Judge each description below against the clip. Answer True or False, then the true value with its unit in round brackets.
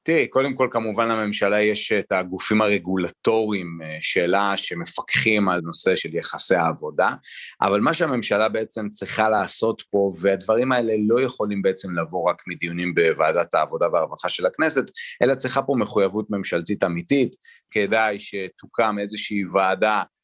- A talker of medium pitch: False (105 Hz)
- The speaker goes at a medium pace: True (135 wpm)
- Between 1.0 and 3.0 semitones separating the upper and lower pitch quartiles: True (2.7 semitones)